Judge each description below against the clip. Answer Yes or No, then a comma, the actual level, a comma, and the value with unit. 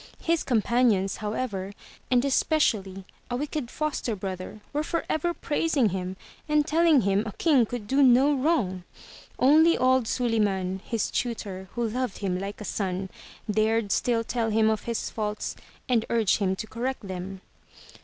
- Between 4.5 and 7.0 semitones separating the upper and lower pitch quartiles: Yes, average, 4.8 semitones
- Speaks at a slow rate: No, average, 155 wpm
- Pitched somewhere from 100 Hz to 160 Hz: No, high, 225 Hz